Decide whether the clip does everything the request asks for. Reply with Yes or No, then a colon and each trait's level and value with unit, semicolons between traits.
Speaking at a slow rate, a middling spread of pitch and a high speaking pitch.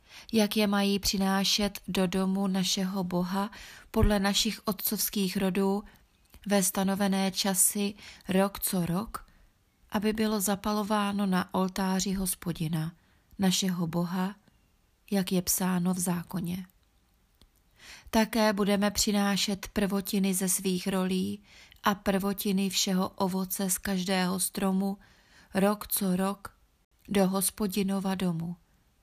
No: slow, 105 wpm; narrow, 1.4 semitones; high, 195 Hz